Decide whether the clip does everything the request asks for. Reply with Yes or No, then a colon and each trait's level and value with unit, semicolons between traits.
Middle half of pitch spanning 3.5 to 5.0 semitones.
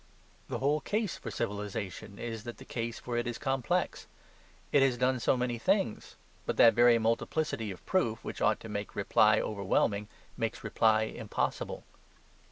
No: average, 3.0 semitones